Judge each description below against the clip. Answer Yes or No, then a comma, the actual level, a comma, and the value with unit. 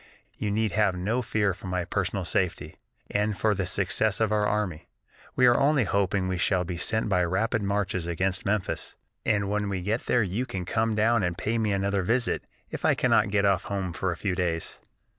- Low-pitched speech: Yes, low, 100 Hz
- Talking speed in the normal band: No, fast, 210 wpm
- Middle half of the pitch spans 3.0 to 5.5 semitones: No, narrow, 2.6 semitones